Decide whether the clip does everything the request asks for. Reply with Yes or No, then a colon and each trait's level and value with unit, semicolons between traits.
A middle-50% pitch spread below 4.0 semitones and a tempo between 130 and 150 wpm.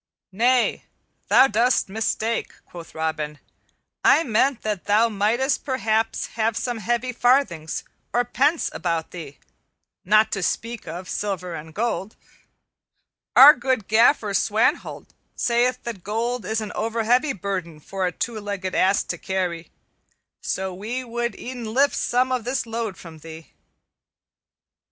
No: average, 4.4 semitones; slow, 135 wpm